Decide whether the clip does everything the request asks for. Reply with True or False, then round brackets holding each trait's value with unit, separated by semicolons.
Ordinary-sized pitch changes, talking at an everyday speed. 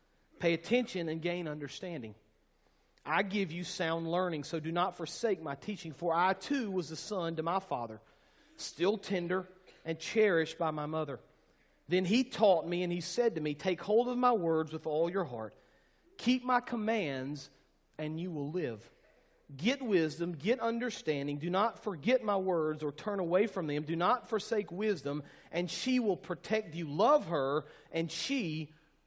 True (4.8 semitones; 175 wpm)